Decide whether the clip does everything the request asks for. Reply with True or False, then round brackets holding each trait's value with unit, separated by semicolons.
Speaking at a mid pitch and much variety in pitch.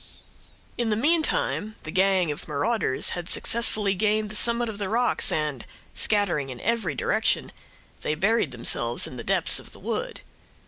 False (200 Hz; 6.7 semitones)